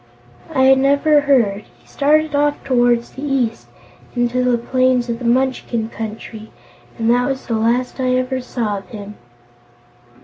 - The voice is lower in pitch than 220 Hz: No, very high, 250 Hz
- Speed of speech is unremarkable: Yes, average, 150 wpm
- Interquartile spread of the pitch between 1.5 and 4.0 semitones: Yes, narrow, 2.4 semitones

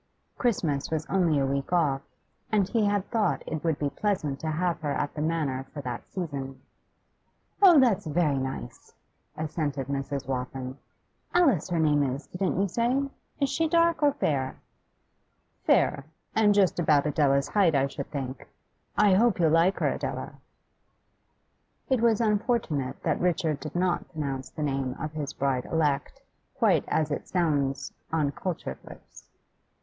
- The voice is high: No, medium, 155 Hz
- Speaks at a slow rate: No, average, 155 wpm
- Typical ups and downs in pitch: No, wide, 5.7 semitones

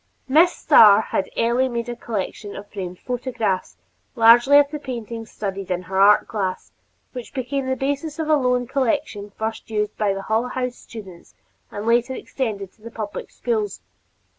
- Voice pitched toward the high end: Yes, high, 230 Hz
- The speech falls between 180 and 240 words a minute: No, average, 170 wpm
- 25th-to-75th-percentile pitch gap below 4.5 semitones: Yes, average, 4.1 semitones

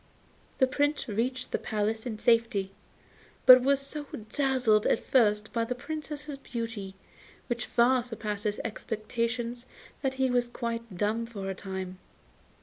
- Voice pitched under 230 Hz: No, high, 235 Hz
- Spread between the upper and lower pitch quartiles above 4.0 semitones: No, average, 3.3 semitones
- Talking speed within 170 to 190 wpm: No, average, 145 wpm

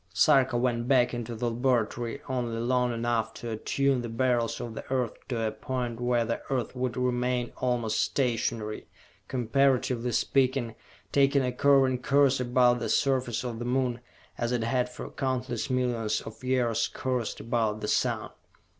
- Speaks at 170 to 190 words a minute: No, average, 160 wpm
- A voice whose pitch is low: Yes, low, 125 Hz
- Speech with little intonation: Yes, narrow, 1.7 semitones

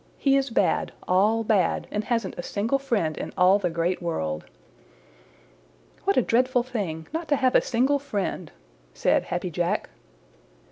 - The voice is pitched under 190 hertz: No, high, 215 Hz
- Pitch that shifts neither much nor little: No, wide, 6.3 semitones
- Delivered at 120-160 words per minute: Yes, average, 155 wpm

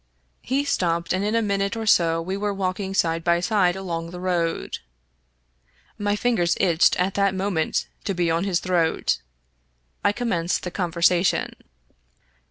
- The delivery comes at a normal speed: Yes, average, 155 wpm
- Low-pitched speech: No, medium, 185 Hz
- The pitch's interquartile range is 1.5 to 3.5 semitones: Yes, average, 2.7 semitones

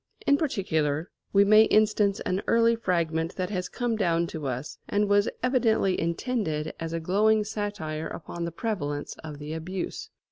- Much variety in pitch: No, average, 4.9 semitones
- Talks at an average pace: Yes, average, 165 wpm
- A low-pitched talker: No, medium, 185 Hz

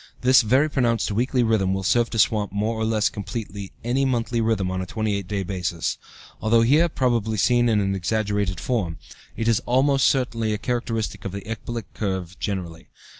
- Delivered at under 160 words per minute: No, average, 180 wpm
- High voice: No, low, 110 Hz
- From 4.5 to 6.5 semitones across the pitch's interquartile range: No, average, 3.4 semitones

